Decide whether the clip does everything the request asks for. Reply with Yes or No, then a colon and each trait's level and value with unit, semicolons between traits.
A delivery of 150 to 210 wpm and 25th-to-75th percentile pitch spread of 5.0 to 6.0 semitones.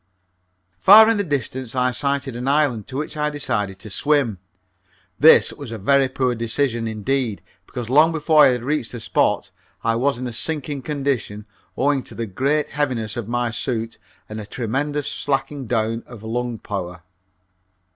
No: average, 170 wpm; average, 4.0 semitones